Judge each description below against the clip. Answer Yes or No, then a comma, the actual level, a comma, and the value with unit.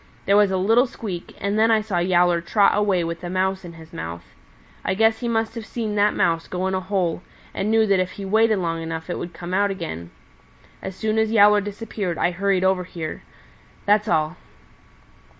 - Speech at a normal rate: No, fast, 210 wpm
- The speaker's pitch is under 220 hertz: Yes, high, 190 Hz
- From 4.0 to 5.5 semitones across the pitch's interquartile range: No, average, 3.3 semitones